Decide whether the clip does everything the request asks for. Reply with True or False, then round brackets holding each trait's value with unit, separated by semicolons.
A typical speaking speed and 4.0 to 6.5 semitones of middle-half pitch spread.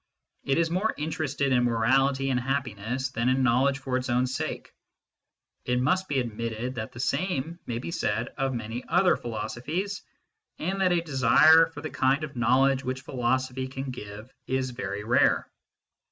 False (170 wpm; 3.0 semitones)